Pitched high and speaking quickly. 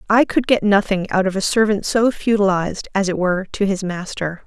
Yes: high, 200 Hz; fast, 215 wpm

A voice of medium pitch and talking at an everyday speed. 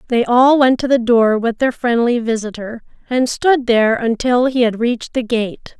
No: high, 240 Hz; average, 195 wpm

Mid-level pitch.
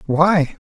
Yes: medium, 165 Hz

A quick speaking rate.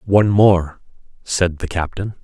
No: slow, 135 wpm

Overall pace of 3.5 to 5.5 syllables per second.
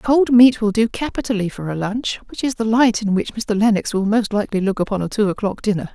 No: 5.8 syllables/s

